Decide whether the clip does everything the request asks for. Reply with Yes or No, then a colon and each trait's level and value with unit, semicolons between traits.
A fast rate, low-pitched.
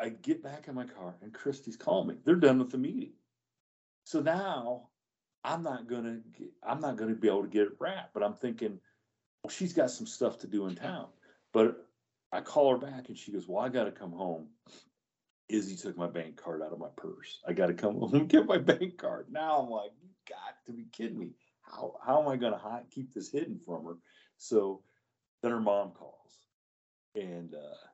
Yes: fast, 215 wpm; low, 115 Hz